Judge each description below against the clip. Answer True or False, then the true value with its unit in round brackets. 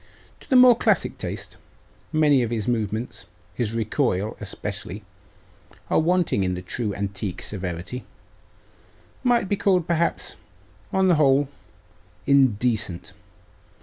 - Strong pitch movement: True (8.2 semitones)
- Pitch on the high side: False (120 Hz)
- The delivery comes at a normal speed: False (115 wpm)